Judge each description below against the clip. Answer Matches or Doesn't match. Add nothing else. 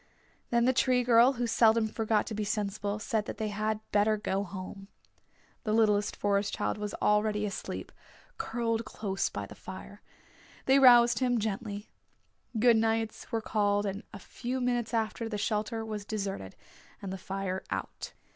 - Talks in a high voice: Matches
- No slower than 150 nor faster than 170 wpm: Matches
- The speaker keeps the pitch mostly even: Matches